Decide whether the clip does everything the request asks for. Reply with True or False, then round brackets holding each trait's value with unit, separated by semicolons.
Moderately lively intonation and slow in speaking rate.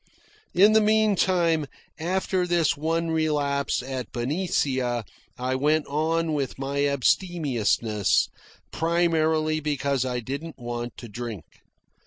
True (4.3 semitones; 110 wpm)